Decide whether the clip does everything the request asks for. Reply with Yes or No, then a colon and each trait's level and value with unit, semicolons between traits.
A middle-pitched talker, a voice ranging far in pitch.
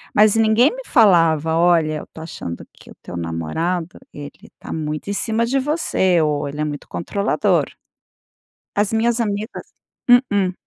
Yes: medium, 180 Hz; wide, 6.4 semitones